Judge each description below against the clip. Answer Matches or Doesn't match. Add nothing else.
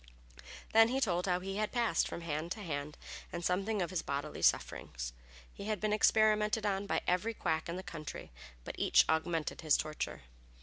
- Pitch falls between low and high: Matches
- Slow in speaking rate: Doesn't match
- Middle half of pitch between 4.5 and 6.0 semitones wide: Matches